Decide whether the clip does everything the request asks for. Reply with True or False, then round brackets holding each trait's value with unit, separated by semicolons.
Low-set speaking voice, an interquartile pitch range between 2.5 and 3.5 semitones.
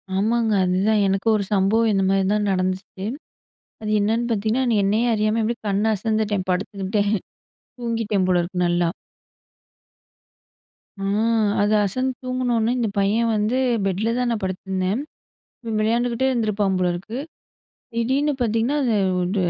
False (215 Hz; 3.0 semitones)